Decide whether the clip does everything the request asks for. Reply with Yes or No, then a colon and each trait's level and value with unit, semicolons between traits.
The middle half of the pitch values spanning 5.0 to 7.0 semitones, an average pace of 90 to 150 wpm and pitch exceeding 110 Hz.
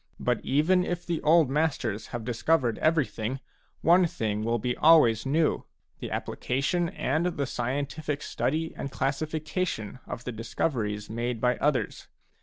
Yes: wide, 5.4 semitones; average, 145 wpm; medium, 140 Hz